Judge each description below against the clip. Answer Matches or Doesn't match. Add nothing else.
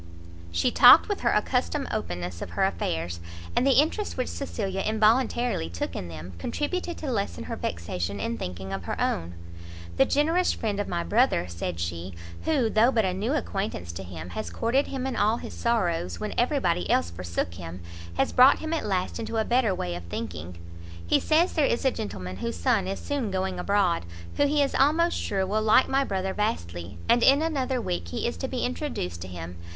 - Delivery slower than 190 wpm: Doesn't match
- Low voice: Doesn't match